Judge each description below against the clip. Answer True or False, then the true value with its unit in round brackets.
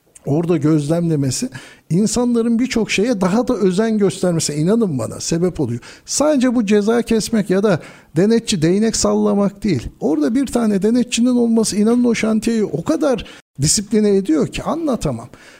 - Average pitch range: True (4.9 semitones)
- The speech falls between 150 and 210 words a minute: False (140 wpm)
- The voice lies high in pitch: True (210 Hz)